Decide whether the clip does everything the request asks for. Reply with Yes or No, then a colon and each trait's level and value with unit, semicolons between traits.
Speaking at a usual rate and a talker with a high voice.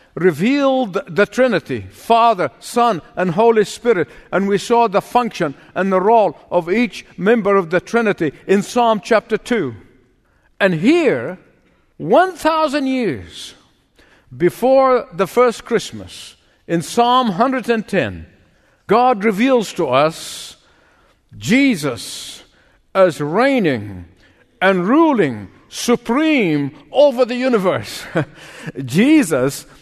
No: slow, 105 wpm; high, 205 Hz